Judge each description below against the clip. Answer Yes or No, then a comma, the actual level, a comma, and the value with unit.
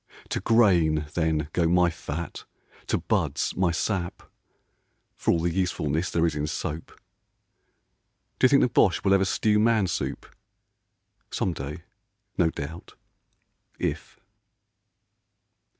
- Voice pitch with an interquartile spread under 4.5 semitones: Yes, average, 3.3 semitones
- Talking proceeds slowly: Yes, slow, 120 wpm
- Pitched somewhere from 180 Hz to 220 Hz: No, very low, 85 Hz